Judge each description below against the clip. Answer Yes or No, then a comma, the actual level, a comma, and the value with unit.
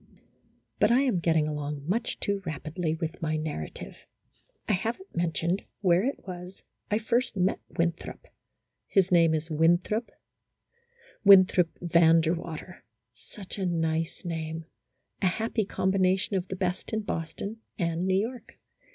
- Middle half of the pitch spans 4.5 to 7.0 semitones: No, average, 3.2 semitones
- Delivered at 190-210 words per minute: No, average, 145 wpm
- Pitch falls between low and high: Yes, medium, 175 Hz